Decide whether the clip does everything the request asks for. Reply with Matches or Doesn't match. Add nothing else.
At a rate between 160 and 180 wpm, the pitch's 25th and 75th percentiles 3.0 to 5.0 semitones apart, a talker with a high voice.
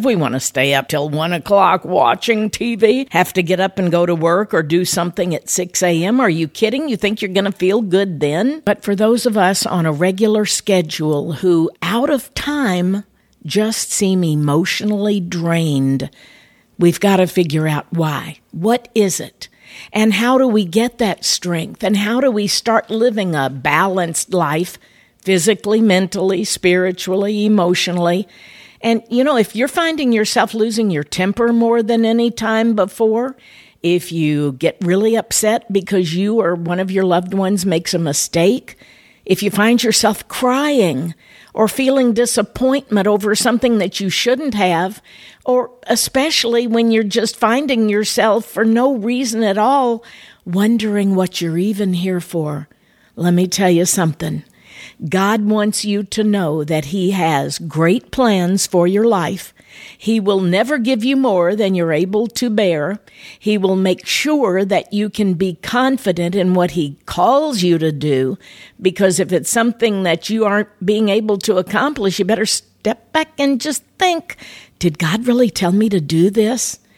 Matches